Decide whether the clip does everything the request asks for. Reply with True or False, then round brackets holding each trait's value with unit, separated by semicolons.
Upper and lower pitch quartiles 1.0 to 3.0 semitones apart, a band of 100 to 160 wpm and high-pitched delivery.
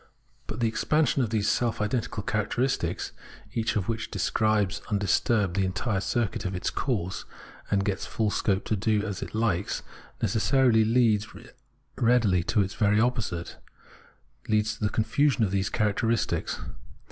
False (2.6 semitones; 150 wpm; 110 Hz)